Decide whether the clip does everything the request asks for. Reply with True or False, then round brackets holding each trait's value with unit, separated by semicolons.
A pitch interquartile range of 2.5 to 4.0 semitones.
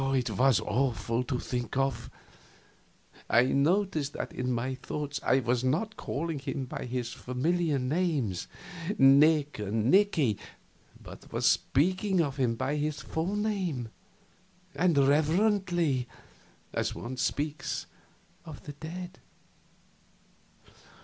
False (4.8 semitones)